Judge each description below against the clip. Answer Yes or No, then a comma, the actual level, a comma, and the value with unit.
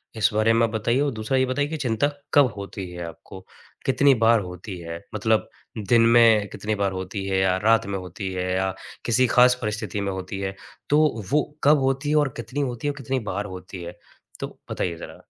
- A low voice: Yes, low, 110 Hz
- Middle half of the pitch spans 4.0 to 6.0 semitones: Yes, average, 5.2 semitones